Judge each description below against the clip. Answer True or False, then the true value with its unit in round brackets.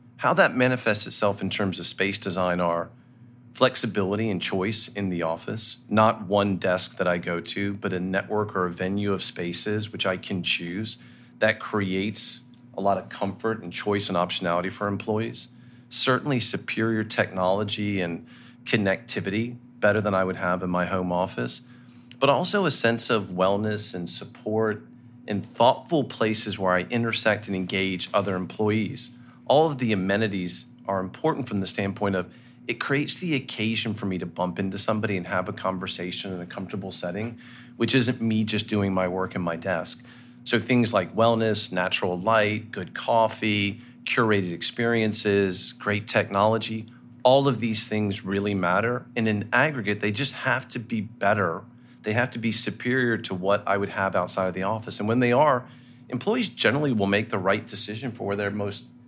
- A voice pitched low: True (105 Hz)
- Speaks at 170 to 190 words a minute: True (175 wpm)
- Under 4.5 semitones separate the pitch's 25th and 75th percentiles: True (3.9 semitones)